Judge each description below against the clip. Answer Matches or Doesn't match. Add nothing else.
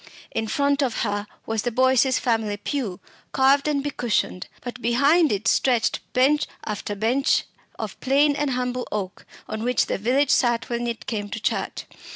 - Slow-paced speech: Doesn't match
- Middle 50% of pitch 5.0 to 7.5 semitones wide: Doesn't match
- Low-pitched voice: Doesn't match